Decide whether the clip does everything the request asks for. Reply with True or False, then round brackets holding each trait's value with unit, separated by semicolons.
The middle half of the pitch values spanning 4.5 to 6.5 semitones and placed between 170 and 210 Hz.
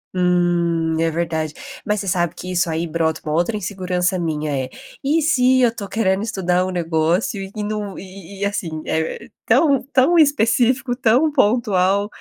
True (5.2 semitones; 185 Hz)